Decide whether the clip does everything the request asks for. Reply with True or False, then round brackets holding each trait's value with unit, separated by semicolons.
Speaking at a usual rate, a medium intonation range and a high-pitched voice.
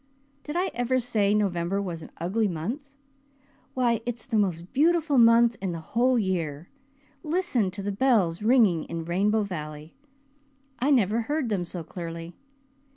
False (155 wpm; 6.0 semitones; 210 Hz)